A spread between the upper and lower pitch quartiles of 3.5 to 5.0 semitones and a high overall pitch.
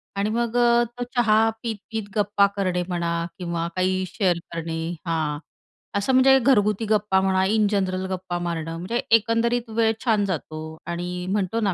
Yes: average, 4.1 semitones; high, 200 Hz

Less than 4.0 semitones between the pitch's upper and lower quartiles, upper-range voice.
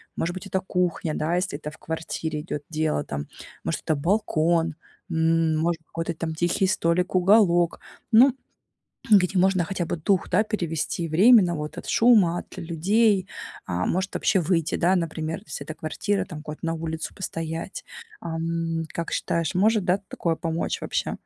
No: narrow, 2.6 semitones; medium, 170 Hz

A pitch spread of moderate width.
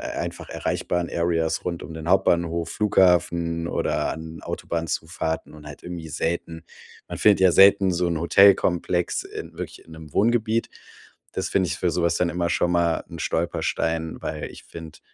No: narrow, 1.6 semitones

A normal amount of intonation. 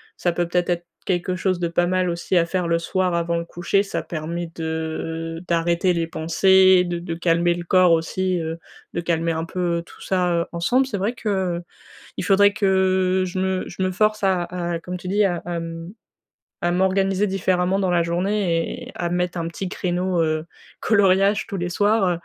No: narrow, 1.9 semitones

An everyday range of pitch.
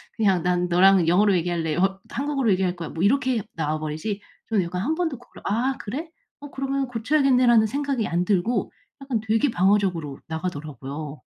No: wide, 6.5 semitones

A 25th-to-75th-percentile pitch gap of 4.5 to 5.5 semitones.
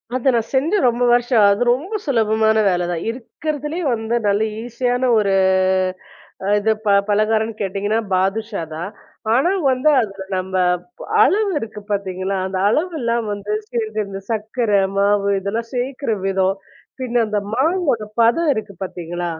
No: average, 3.8 semitones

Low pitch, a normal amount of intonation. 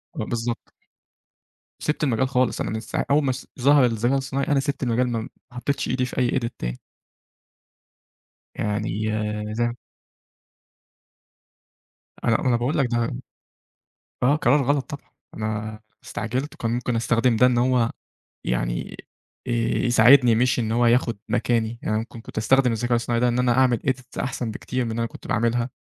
No: low, 120 Hz; narrow, 2.0 semitones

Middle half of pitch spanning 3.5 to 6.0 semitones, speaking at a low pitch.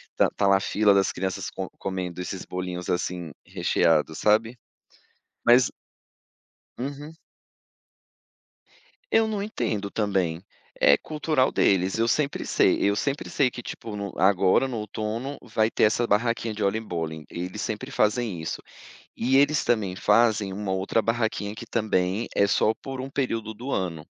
Yes: average, 4.1 semitones; low, 105 Hz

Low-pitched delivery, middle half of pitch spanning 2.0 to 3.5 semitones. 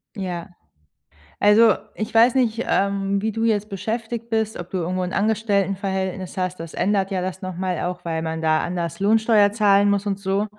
No: high, 195 Hz; average, 2.9 semitones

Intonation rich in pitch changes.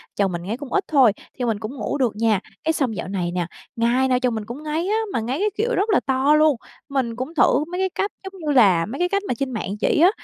Yes: wide, 5.7 semitones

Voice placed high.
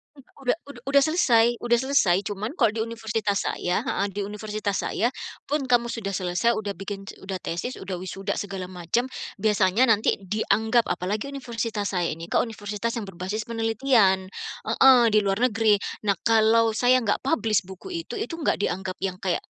Yes: high, 215 Hz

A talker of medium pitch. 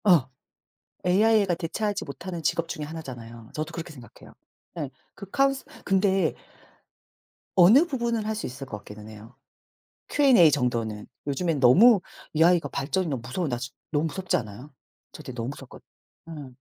Yes: medium, 160 Hz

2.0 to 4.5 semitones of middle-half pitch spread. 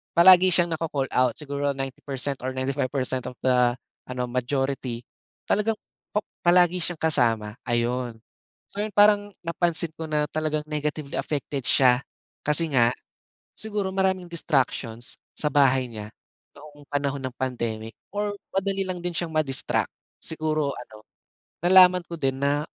No: average, 5.0 semitones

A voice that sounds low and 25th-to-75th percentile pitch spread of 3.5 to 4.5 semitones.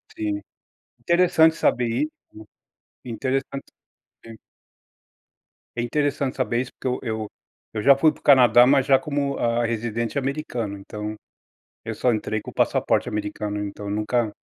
Yes: low, 120 Hz; average, 4.2 semitones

